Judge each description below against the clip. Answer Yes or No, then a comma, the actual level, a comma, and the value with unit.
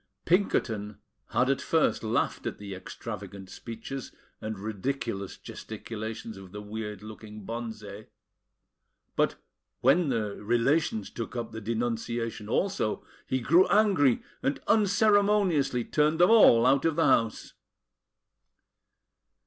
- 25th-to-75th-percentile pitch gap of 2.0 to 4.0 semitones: No, wide, 5.5 semitones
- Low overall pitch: Yes, low, 115 Hz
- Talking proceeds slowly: Yes, slow, 115 wpm